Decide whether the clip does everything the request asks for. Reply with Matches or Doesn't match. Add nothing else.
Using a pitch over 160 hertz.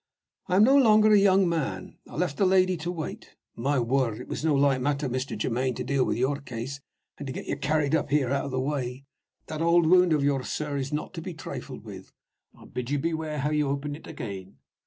Doesn't match